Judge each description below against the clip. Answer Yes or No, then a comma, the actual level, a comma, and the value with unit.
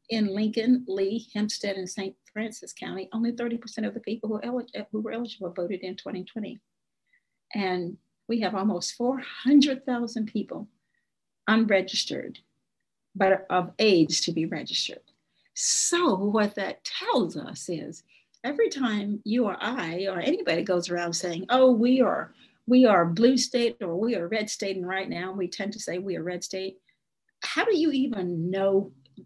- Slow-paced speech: No, average, 155 wpm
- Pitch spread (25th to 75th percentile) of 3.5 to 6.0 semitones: Yes, average, 4.3 semitones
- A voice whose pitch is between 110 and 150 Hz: No, high, 210 Hz